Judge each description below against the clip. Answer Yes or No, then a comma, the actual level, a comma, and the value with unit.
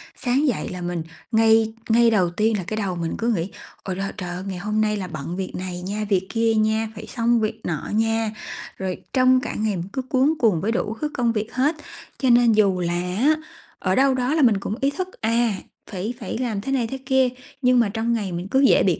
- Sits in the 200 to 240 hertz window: Yes, high, 220 Hz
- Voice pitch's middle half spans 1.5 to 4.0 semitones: No, average, 4.4 semitones